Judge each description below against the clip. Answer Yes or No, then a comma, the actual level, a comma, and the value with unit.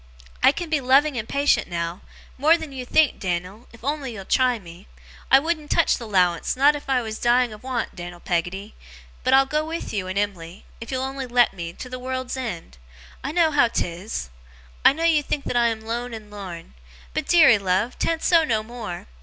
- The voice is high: Yes, high, 240 Hz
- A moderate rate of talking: No, fast, 210 wpm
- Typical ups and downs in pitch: No, wide, 5.8 semitones